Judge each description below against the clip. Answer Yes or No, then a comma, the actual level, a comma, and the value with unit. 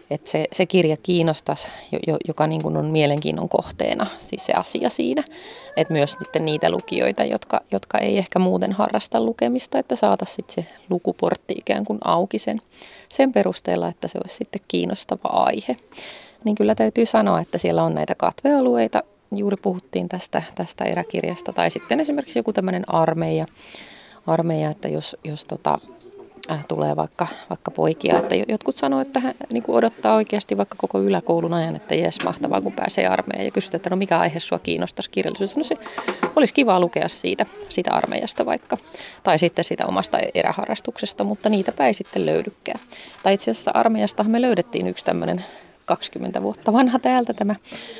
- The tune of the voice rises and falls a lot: Yes, wide, 6.6 semitones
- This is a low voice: No, medium, 180 Hz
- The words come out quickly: Yes, fast, 160 wpm